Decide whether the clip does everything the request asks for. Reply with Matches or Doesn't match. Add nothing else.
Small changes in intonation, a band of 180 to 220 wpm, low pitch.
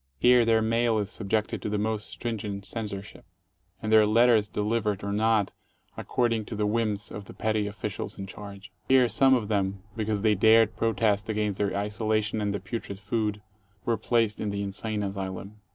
Matches